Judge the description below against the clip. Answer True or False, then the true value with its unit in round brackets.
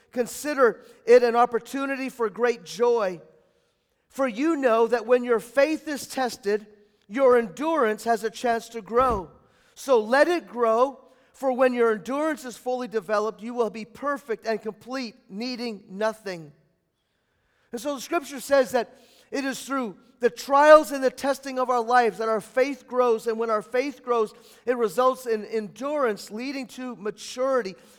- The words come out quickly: False (160 wpm)